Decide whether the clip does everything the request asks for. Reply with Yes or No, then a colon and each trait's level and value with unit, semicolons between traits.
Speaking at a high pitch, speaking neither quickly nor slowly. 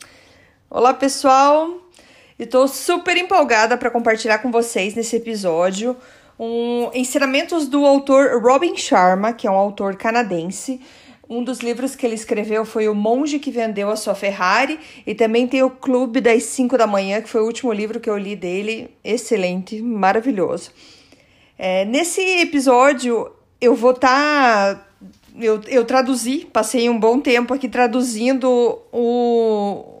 Yes: high, 240 Hz; average, 145 wpm